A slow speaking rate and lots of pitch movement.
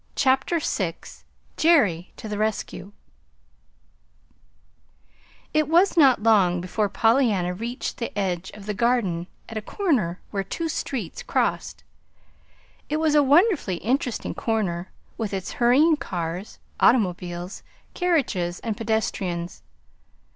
Yes: slow, 115 wpm; wide, 6.9 semitones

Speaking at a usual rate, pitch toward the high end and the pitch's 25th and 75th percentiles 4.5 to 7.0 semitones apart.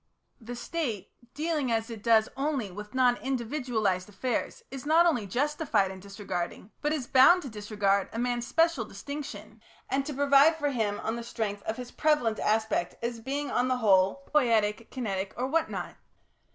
Yes: average, 175 wpm; high, 240 Hz; average, 5.1 semitones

